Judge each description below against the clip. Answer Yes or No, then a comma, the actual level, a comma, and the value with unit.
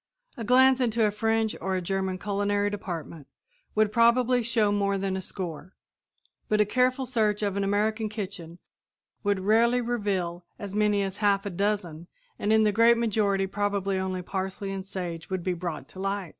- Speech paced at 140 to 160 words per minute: No, average, 180 wpm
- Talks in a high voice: Yes, high, 205 Hz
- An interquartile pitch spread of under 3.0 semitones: Yes, narrow, 2.4 semitones